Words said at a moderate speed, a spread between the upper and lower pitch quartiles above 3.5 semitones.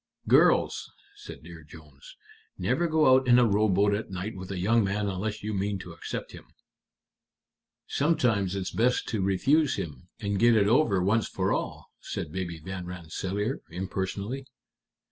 Yes: average, 160 wpm; average, 3.9 semitones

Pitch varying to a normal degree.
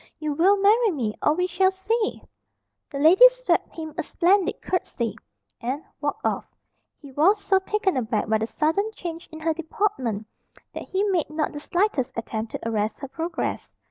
No: wide, 6.5 semitones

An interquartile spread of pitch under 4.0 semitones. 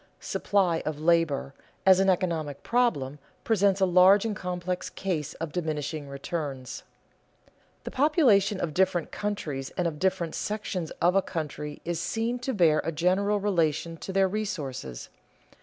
No: average, 4.3 semitones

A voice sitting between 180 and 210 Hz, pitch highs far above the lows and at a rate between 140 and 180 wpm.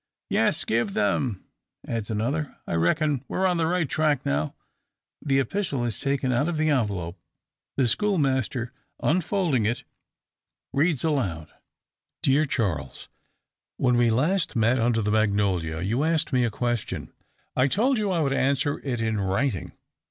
No: low, 130 Hz; wide, 5.8 semitones; average, 150 wpm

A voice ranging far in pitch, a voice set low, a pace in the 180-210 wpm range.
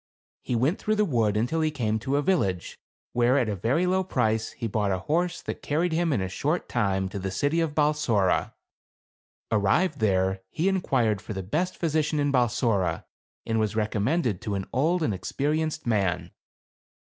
Yes: wide, 7.3 semitones; low, 120 Hz; average, 185 wpm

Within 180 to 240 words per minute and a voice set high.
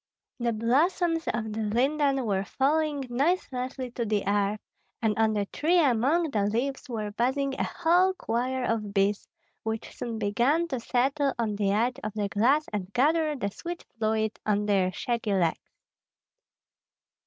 No: average, 155 wpm; high, 235 Hz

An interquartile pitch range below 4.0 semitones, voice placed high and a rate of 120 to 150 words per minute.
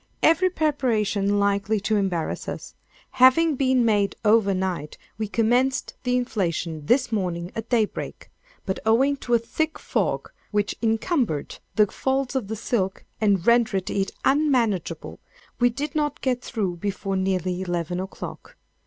No: average, 4.8 semitones; high, 220 Hz; average, 145 wpm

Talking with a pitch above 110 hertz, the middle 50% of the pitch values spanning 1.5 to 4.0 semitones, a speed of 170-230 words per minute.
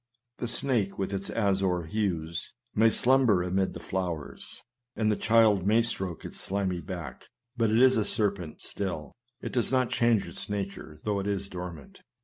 No: low, 100 Hz; average, 3.6 semitones; average, 175 wpm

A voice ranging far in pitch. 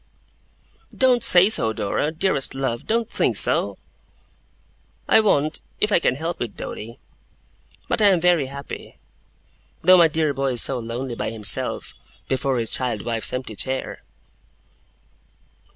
Yes: wide, 6.6 semitones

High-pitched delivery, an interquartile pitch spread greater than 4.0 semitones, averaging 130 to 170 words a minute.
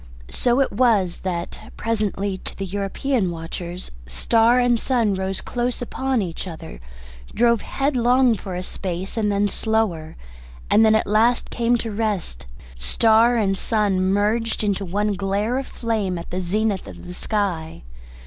No: high, 205 Hz; average, 3.7 semitones; average, 150 wpm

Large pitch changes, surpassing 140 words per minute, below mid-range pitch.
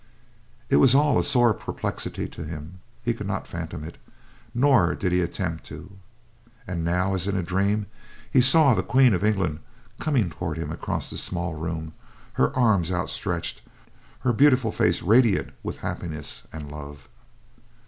Yes: wide, 5.7 semitones; average, 160 wpm; very low, 90 Hz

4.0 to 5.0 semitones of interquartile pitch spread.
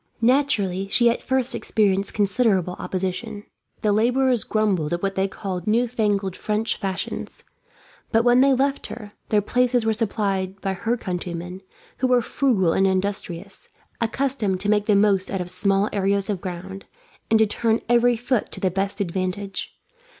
No: average, 3.5 semitones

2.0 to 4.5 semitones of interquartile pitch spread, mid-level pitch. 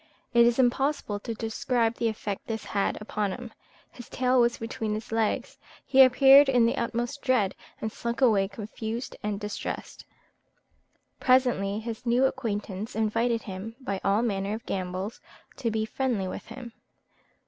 No: average, 2.8 semitones; high, 225 Hz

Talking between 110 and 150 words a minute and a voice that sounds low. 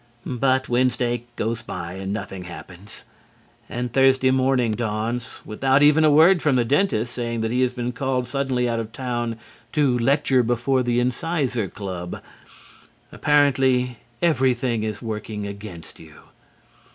Yes: average, 140 wpm; low, 125 Hz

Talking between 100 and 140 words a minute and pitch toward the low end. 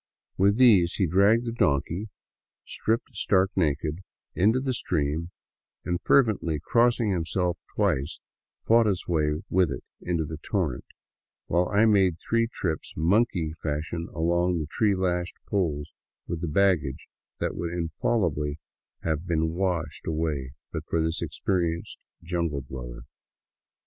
Yes: slow, 135 wpm; very low, 85 Hz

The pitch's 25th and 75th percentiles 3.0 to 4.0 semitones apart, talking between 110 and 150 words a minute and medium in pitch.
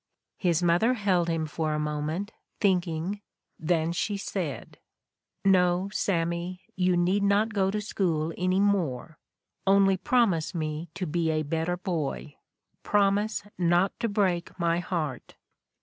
Yes: average, 3.3 semitones; slow, 135 wpm; medium, 180 Hz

